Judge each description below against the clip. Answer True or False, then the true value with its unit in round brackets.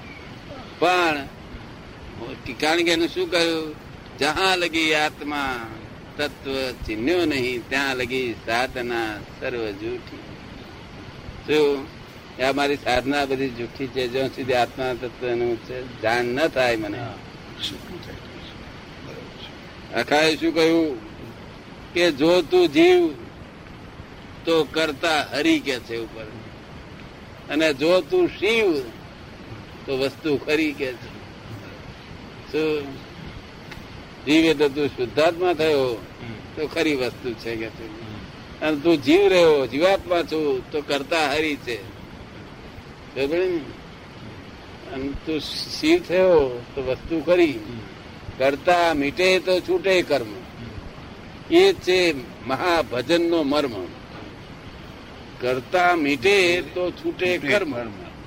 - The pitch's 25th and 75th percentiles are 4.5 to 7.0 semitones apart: True (5.3 semitones)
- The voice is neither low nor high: True (150 Hz)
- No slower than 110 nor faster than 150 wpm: False (75 wpm)